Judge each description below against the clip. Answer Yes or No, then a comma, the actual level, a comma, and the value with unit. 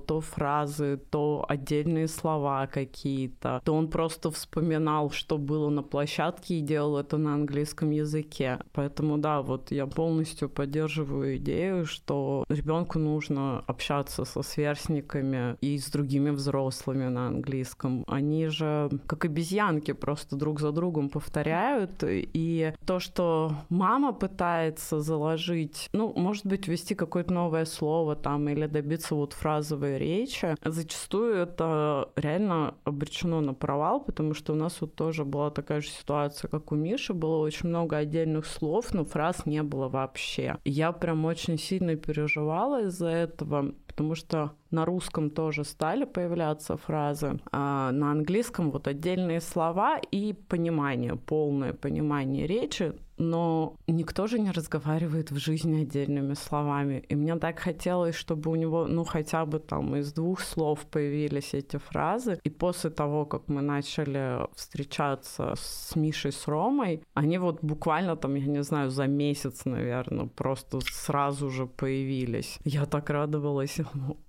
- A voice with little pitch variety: Yes, narrow, 2.3 semitones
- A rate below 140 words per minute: No, average, 145 wpm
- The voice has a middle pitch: Yes, medium, 155 Hz